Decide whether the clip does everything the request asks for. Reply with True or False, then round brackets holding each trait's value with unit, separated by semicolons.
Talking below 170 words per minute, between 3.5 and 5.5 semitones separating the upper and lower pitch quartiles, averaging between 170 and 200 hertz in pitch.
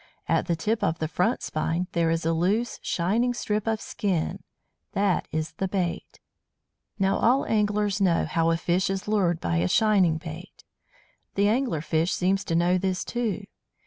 False (175 wpm; 4.0 semitones; 185 Hz)